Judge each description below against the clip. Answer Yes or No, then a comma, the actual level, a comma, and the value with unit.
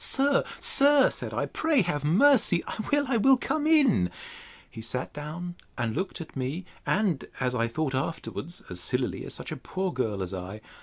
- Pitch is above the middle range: No, medium, 165 Hz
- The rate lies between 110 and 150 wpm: No, average, 190 wpm